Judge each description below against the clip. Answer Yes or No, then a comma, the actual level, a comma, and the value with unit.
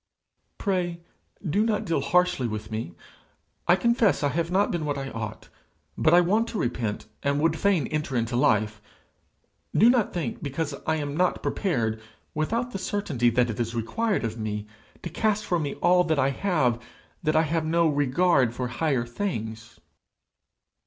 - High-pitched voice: No, medium, 155 Hz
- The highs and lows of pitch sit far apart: Yes, wide, 6.9 semitones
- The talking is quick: No, average, 170 wpm